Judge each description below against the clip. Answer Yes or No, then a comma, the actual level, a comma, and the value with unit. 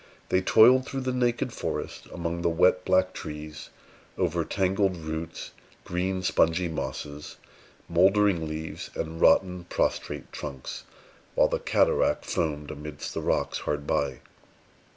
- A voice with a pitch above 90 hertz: No, very low, 85 Hz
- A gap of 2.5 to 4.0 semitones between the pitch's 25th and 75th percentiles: Yes, average, 3.3 semitones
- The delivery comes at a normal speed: No, slow, 130 wpm